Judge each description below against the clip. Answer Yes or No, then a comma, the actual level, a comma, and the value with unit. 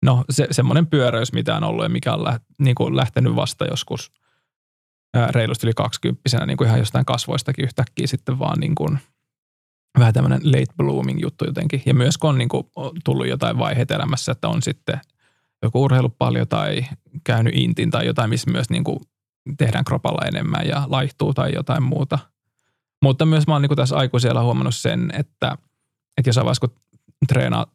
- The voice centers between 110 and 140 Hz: Yes, low, 130 Hz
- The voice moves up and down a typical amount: Yes, average, 3.6 semitones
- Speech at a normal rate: No, fast, 180 wpm